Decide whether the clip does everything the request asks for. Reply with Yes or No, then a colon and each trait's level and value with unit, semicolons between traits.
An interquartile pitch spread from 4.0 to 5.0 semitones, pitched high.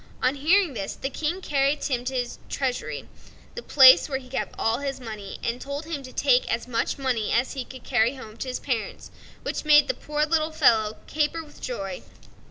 No: average, 3.5 semitones; very high, 265 Hz